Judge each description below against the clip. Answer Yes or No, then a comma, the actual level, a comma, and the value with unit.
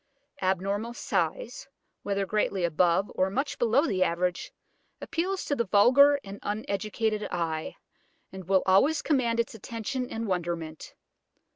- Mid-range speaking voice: No, high, 205 Hz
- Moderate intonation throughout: Yes, average, 4.3 semitones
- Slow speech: Yes, slow, 130 wpm